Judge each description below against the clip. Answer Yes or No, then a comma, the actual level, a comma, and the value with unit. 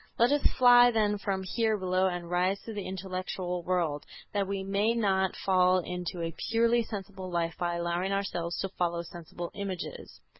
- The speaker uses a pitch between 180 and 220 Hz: Yes, high, 190 Hz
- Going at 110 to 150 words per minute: No, average, 175 wpm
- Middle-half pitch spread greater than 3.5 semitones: No, narrow, 2.4 semitones